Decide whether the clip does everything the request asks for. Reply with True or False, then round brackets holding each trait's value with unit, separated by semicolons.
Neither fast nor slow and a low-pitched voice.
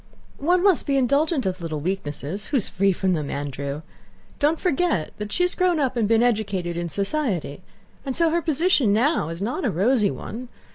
False (195 wpm; 225 Hz)